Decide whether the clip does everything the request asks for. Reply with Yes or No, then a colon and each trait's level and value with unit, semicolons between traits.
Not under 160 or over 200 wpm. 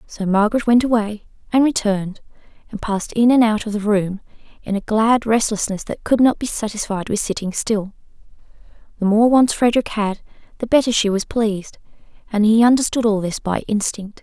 Yes: average, 180 wpm